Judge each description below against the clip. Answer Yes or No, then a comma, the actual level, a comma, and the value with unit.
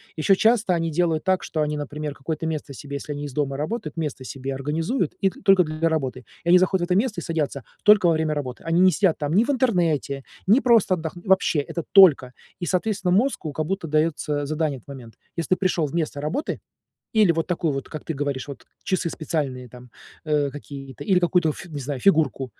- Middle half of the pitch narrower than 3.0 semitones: No, average, 4.1 semitones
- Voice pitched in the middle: Yes, medium, 155 Hz